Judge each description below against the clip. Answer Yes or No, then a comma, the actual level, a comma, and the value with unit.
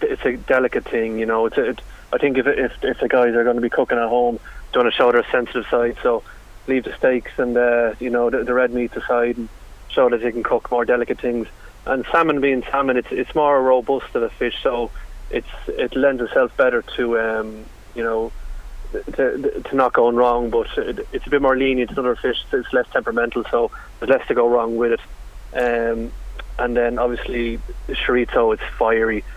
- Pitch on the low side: Yes, low, 120 Hz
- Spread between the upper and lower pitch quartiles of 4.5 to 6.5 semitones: No, narrow, 2.5 semitones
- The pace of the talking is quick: Yes, fast, 220 wpm